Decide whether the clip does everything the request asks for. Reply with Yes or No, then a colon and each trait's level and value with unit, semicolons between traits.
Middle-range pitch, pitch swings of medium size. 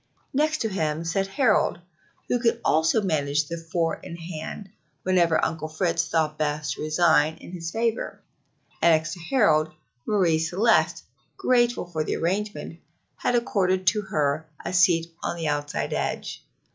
Yes: medium, 170 Hz; average, 4.0 semitones